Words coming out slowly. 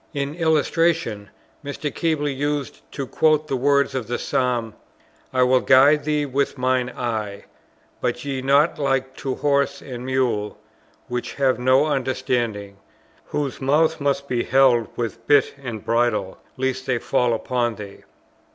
No: average, 145 wpm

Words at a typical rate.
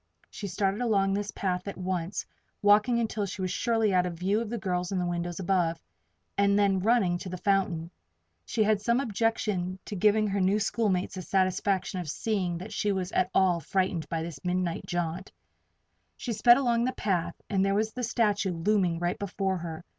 Yes: average, 195 wpm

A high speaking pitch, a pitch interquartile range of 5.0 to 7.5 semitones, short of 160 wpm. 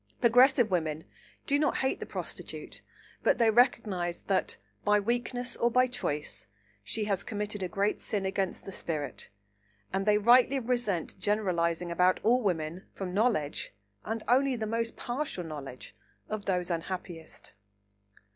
Yes: high, 205 Hz; average, 5.3 semitones; average, 145 wpm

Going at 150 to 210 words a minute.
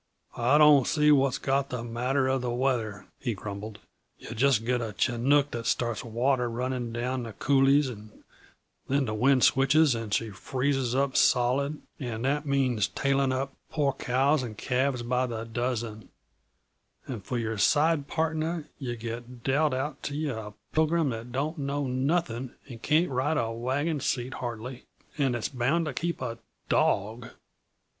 Yes: average, 165 wpm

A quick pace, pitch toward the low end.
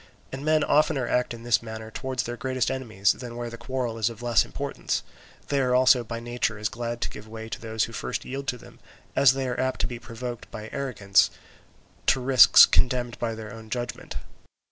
Yes: fast, 210 wpm; low, 120 Hz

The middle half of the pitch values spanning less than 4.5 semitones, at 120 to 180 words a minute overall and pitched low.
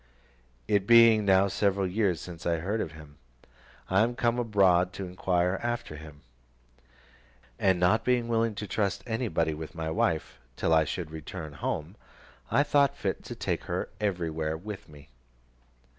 No: average, 5.3 semitones; average, 160 wpm; very low, 95 Hz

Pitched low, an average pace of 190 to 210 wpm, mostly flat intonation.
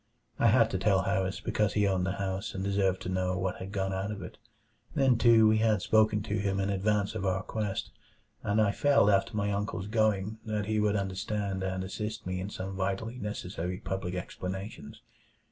Yes: low, 100 Hz; average, 200 wpm; narrow, 2.0 semitones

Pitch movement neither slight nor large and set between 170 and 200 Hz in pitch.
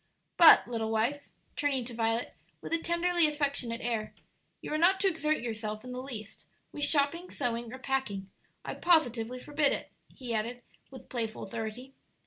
No: average, 4.5 semitones; very high, 250 Hz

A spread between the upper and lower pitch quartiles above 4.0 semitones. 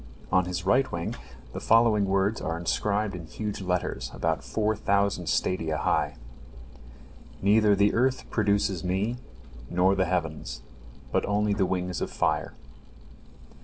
No: average, 2.7 semitones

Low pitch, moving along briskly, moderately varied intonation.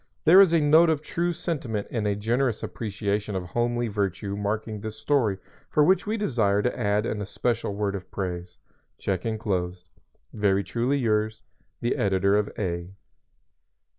No: low, 105 Hz; average, 160 wpm; average, 3.6 semitones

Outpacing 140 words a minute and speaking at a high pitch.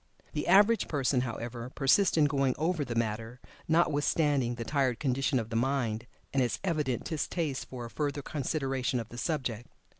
No: average, 170 wpm; low, 135 Hz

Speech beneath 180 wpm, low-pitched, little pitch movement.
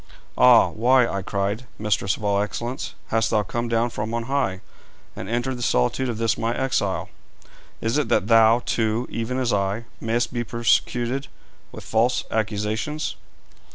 Yes: average, 160 wpm; low, 115 Hz; narrow, 2.3 semitones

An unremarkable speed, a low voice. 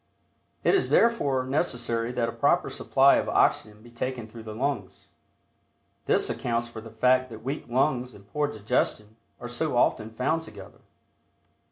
Yes: average, 160 wpm; low, 120 Hz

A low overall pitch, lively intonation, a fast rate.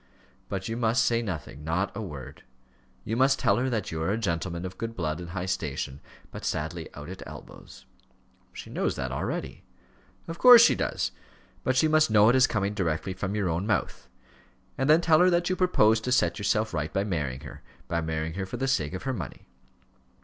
Yes: low, 100 Hz; wide, 6.7 semitones; fast, 210 wpm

